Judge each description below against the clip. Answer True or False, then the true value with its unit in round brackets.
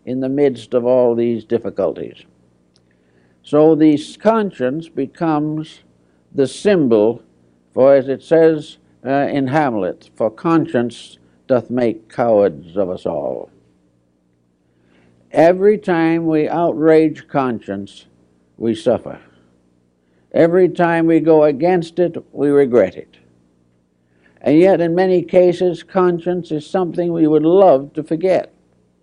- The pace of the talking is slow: True (120 wpm)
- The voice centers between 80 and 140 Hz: True (135 Hz)